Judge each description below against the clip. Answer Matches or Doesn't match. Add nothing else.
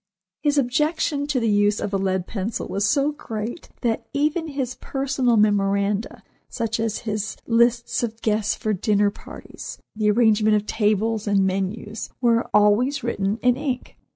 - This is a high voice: Matches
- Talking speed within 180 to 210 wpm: Doesn't match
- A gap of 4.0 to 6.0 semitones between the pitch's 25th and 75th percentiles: Doesn't match